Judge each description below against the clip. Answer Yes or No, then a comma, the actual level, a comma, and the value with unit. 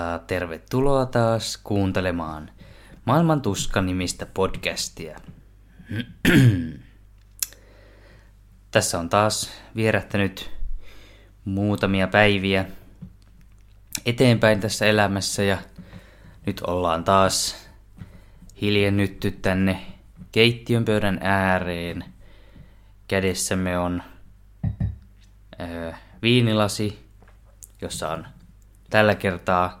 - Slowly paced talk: Yes, slow, 60 wpm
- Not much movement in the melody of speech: Yes, narrow, 1.8 semitones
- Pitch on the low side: Yes, low, 100 Hz